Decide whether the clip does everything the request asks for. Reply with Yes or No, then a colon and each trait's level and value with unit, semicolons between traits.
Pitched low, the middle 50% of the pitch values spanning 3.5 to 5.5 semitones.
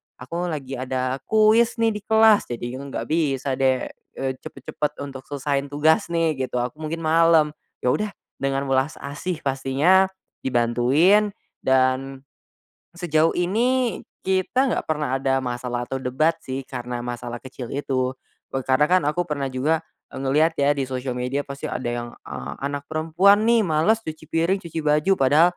No: medium, 145 Hz; average, 4.2 semitones